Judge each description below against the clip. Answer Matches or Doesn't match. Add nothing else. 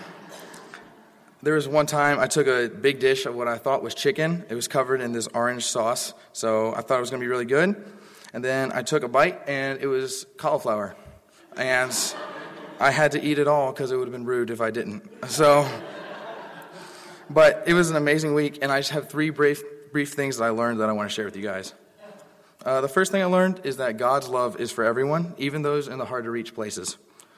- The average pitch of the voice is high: Doesn't match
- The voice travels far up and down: Doesn't match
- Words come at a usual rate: Doesn't match